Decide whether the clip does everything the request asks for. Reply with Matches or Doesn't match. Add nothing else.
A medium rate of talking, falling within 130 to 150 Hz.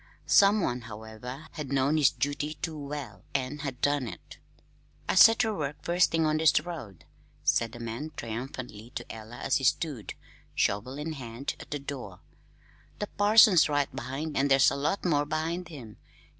Matches